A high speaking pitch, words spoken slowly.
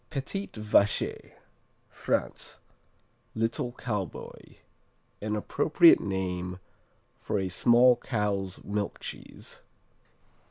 No: low, 105 Hz; slow, 80 wpm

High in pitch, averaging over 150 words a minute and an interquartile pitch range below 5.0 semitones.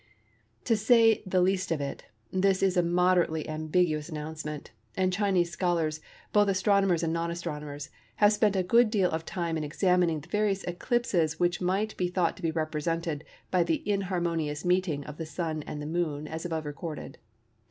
No: medium, 175 Hz; average, 175 wpm; average, 3.1 semitones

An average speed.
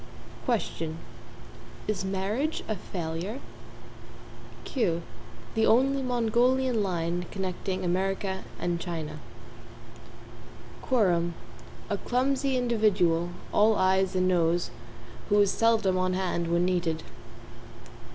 No: slow, 95 wpm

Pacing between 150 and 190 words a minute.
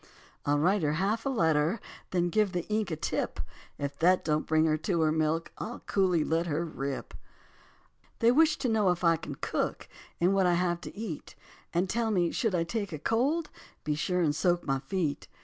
No: fast, 205 wpm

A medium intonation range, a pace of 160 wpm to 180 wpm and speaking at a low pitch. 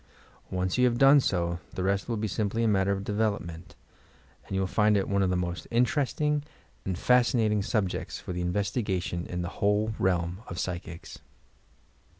Yes: average, 3.4 semitones; average, 175 wpm; low, 100 Hz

